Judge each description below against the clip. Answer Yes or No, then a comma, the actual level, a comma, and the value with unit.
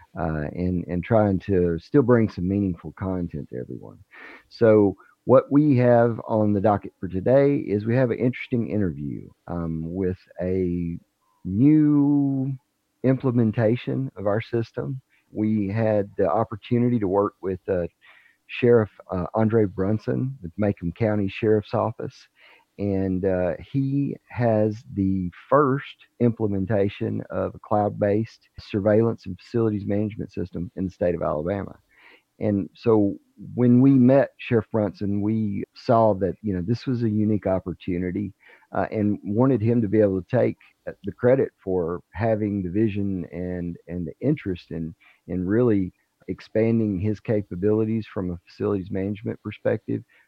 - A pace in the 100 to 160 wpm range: Yes, average, 140 wpm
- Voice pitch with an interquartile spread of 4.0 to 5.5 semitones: No, average, 3.6 semitones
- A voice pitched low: Yes, low, 105 Hz